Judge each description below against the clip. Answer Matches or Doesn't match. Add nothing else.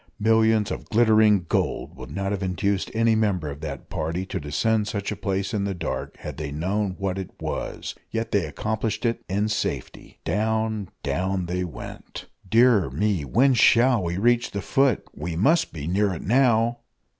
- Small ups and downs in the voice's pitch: Doesn't match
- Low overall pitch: Matches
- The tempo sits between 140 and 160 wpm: Doesn't match